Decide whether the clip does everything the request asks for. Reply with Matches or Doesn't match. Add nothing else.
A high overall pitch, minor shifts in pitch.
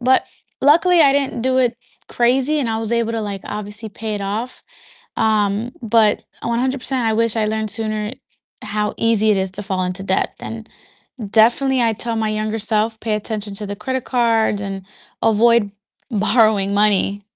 Matches